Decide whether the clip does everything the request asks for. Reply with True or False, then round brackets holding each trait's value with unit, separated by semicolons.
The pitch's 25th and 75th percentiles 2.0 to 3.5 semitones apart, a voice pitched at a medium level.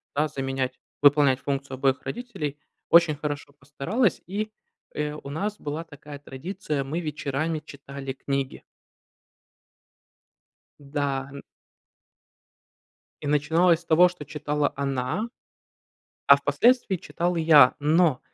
True (3.2 semitones; 145 Hz)